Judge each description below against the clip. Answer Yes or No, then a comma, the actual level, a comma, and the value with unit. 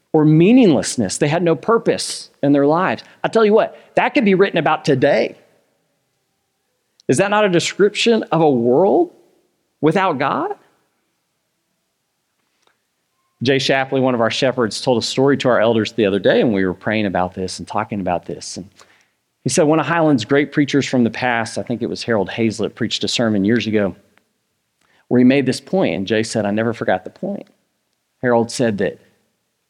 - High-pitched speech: No, low, 135 Hz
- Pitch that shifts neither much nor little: No, wide, 6.7 semitones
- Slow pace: No, average, 185 wpm